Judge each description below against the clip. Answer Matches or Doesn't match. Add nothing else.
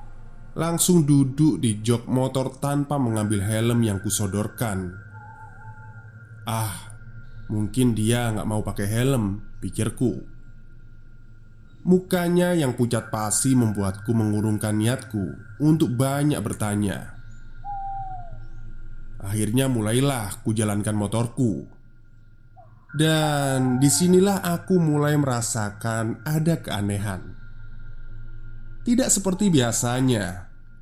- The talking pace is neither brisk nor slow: Doesn't match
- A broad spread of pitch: Doesn't match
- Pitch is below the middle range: Matches